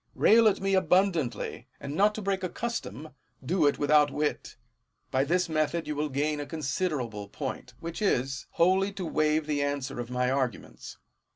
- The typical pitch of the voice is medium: Yes, medium, 150 Hz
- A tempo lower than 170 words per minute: No, average, 175 wpm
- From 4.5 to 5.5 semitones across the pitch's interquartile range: Yes, average, 5.0 semitones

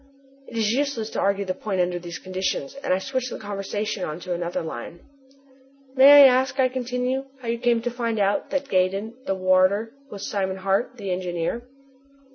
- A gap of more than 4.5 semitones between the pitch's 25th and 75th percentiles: Yes, average, 5.1 semitones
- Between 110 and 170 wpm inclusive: No, average, 195 wpm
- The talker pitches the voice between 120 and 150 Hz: No, high, 210 Hz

